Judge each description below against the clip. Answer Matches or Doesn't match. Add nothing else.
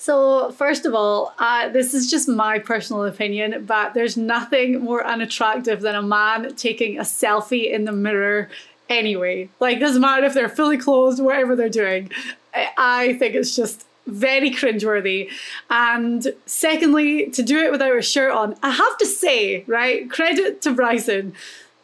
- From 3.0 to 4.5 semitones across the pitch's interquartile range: Matches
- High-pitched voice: Matches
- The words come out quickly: Doesn't match